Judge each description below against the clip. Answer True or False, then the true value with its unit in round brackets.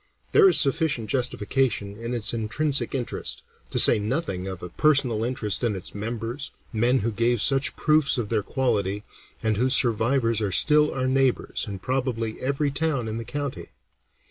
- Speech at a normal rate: True (170 wpm)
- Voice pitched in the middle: False (120 Hz)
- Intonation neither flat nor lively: True (4.1 semitones)